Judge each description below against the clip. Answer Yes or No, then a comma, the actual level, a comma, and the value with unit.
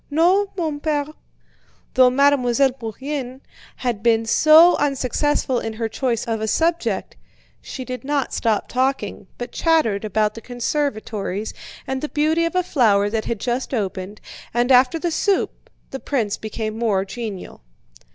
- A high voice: Yes, very high, 250 Hz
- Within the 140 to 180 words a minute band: Yes, average, 150 wpm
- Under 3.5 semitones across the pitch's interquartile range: No, average, 4.8 semitones